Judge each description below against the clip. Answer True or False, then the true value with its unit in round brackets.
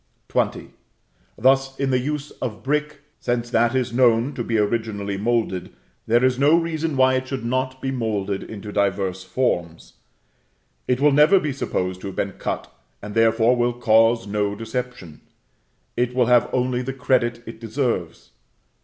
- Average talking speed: True (160 wpm)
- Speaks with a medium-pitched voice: False (120 Hz)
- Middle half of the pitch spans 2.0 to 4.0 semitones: True (3.3 semitones)